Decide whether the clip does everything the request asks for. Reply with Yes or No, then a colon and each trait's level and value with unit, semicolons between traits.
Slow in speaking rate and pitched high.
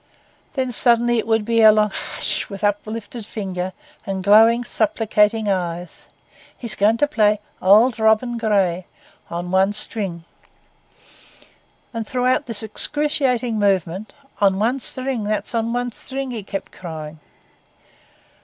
Yes: slow, 125 wpm; high, 215 Hz